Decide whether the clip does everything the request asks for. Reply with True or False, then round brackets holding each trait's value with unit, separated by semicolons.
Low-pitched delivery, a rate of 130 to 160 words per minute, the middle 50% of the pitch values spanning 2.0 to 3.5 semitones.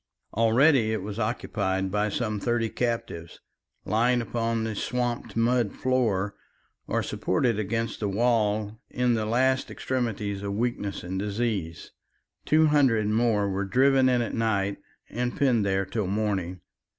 True (110 Hz; 140 wpm; 3.2 semitones)